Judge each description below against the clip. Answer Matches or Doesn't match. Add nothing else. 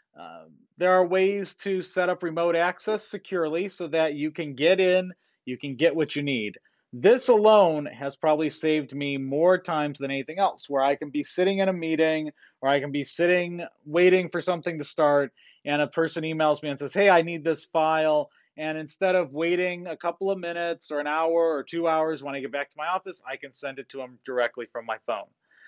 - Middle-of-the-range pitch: Matches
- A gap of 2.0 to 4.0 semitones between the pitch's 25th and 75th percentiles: Matches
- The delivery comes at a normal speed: Doesn't match